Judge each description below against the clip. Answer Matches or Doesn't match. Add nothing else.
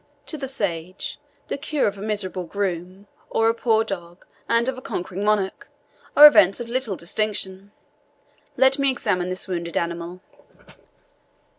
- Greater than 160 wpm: Doesn't match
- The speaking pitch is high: Matches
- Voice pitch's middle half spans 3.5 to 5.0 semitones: Matches